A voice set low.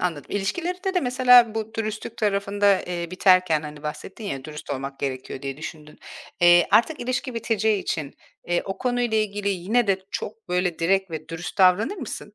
No: high, 195 Hz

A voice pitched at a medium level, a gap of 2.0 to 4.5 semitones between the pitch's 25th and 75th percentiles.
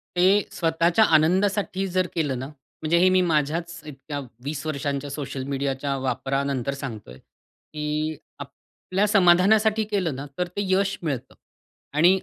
No: medium, 155 Hz; average, 4.9 semitones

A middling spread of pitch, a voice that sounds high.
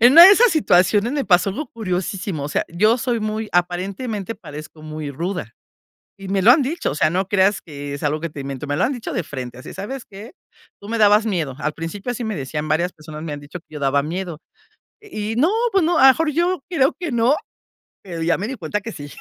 No: wide, 7.3 semitones; high, 195 Hz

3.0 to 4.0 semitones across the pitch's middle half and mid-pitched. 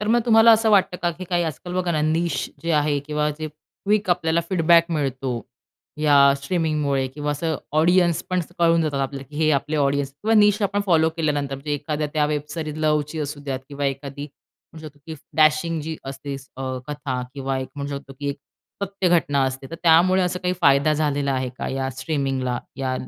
Yes: average, 3.4 semitones; medium, 150 Hz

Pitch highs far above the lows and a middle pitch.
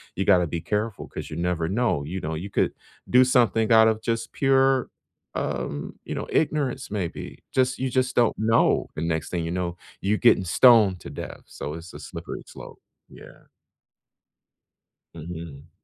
No: wide, 6.2 semitones; low, 100 Hz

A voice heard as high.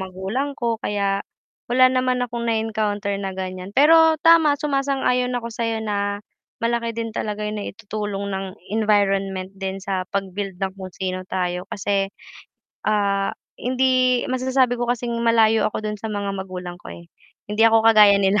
Yes: high, 210 Hz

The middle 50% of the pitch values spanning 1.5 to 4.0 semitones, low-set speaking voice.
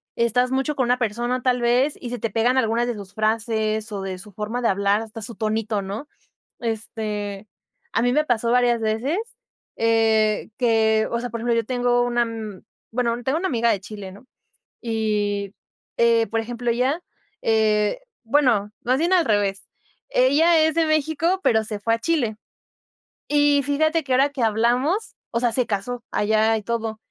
No: average, 2.7 semitones; high, 230 Hz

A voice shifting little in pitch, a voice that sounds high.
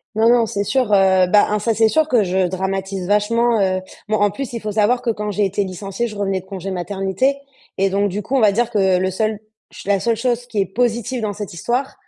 No: average, 3.3 semitones; high, 205 Hz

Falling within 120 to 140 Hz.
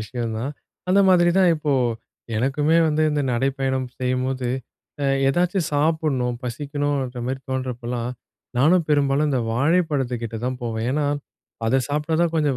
Yes: low, 135 Hz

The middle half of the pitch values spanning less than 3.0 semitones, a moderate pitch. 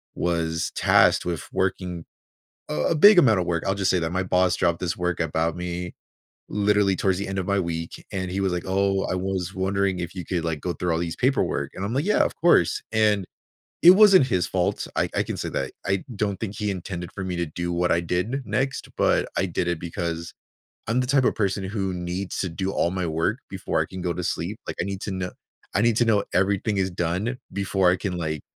No: narrow, 2.4 semitones; very low, 95 Hz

